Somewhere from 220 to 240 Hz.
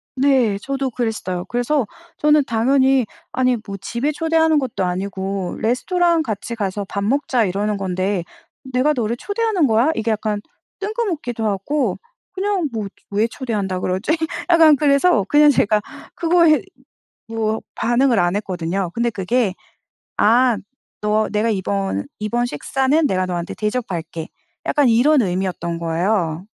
Yes: high, 225 Hz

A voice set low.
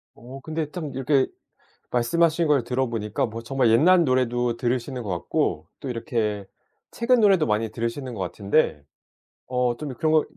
Yes: low, 125 Hz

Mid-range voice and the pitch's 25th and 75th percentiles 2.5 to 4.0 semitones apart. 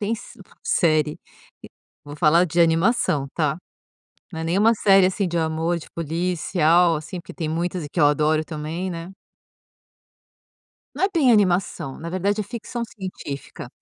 Yes: medium, 170 Hz; average, 3.4 semitones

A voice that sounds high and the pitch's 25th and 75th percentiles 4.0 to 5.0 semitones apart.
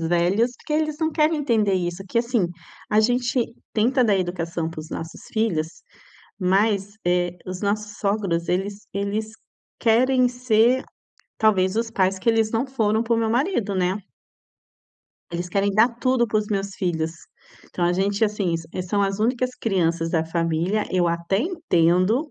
Yes: high, 205 Hz; average, 4.5 semitones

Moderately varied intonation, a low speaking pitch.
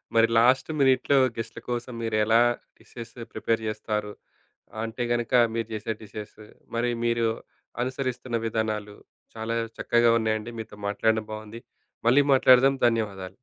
No: narrow, 1.9 semitones; low, 115 Hz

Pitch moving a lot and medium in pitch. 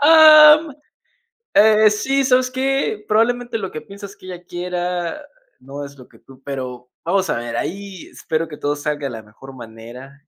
Yes: wide, 8.7 semitones; medium, 180 Hz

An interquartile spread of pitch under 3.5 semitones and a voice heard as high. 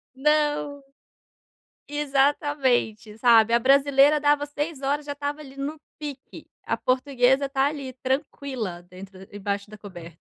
No: average, 3.9 semitones; very high, 275 Hz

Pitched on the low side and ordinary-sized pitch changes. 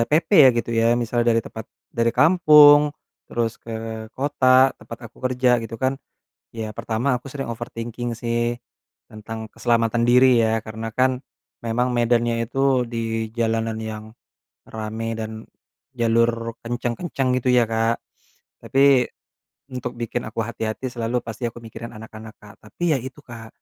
No: low, 115 Hz; narrow, 2.0 semitones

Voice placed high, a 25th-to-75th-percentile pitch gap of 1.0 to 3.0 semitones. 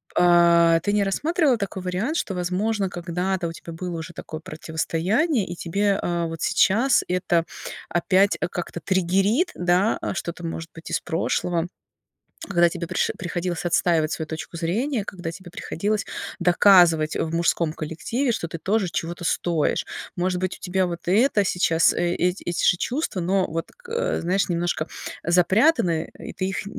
No: medium, 180 Hz; average, 2.7 semitones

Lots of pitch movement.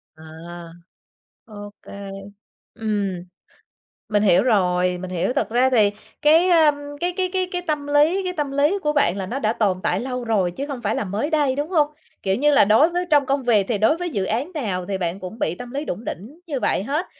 Yes: wide, 7.0 semitones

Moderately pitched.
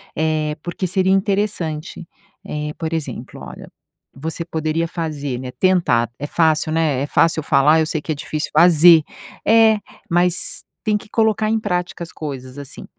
Yes: medium, 160 Hz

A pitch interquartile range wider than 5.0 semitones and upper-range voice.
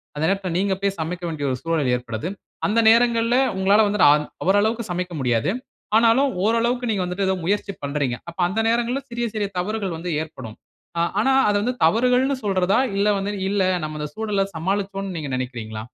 Yes: wide, 5.6 semitones; high, 195 Hz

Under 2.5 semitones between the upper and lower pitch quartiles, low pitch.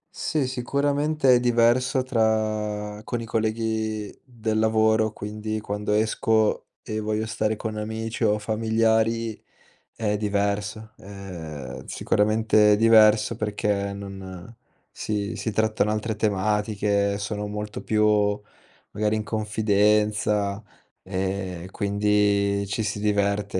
Yes: narrow, 1.3 semitones; low, 105 Hz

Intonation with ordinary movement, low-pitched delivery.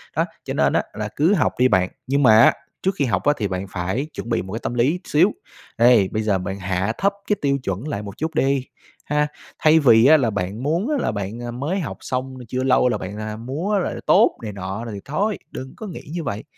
No: wide, 6.3 semitones; low, 125 Hz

